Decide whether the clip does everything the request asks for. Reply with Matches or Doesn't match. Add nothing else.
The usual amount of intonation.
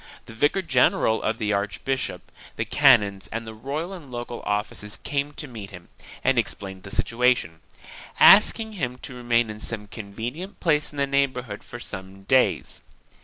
Matches